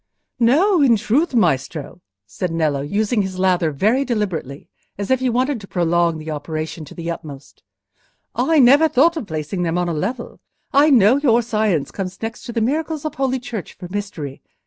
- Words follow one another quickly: No, average, 185 wpm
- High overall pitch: Yes, high, 205 Hz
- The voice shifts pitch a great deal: Yes, wide, 7.5 semitones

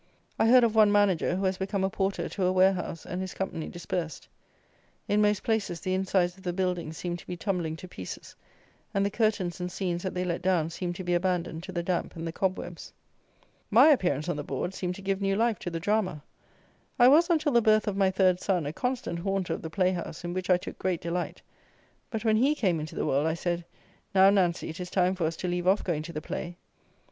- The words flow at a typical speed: No, fast, 235 wpm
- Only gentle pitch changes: Yes, narrow, 2.3 semitones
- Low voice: No, medium, 185 Hz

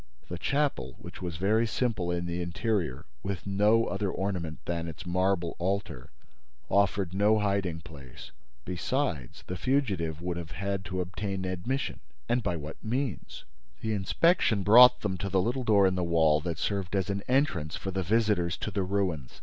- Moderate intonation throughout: Yes, average, 3.5 semitones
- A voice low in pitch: Yes, very low, 95 Hz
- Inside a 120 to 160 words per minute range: No, average, 175 wpm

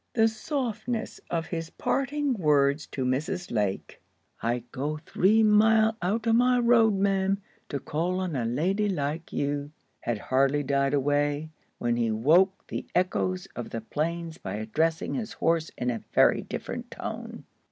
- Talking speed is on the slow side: No, average, 155 wpm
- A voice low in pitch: No, medium, 165 Hz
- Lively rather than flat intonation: Yes, wide, 6.9 semitones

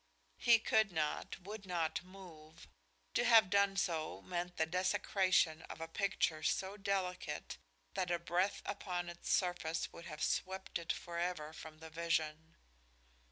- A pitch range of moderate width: Yes, average, 3.0 semitones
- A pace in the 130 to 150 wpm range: Yes, average, 145 wpm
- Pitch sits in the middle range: Yes, medium, 175 Hz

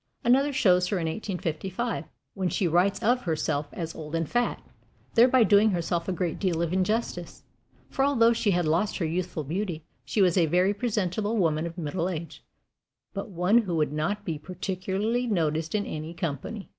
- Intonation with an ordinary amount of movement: Yes, average, 4.2 semitones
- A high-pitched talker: No, medium, 180 Hz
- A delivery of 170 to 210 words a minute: Yes, average, 180 wpm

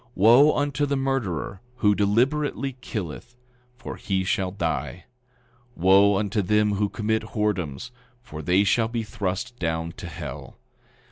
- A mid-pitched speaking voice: No, low, 105 Hz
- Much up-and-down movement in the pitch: No, average, 4.6 semitones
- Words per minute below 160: Yes, average, 145 wpm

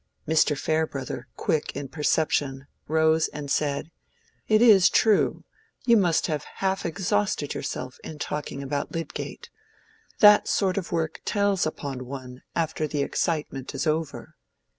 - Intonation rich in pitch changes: No, average, 4.1 semitones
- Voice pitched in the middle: Yes, medium, 155 Hz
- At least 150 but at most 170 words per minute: No, slow, 135 wpm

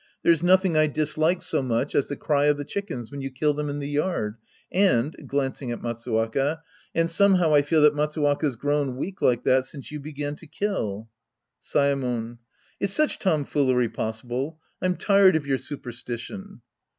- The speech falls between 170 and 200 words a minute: Yes, average, 175 wpm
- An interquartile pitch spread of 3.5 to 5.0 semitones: Yes, average, 3.8 semitones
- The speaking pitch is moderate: Yes, medium, 145 Hz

